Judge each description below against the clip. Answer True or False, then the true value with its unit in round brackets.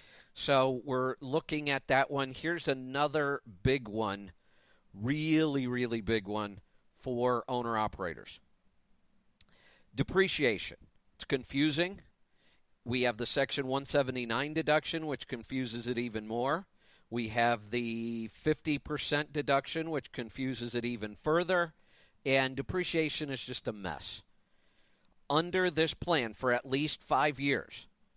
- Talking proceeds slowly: True (115 wpm)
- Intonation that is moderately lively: True (4.0 semitones)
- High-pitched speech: False (135 Hz)